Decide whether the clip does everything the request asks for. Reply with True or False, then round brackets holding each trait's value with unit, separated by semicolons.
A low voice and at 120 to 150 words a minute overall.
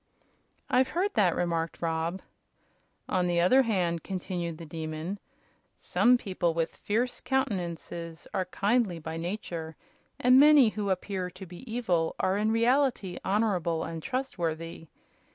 False (185 Hz; 135 wpm)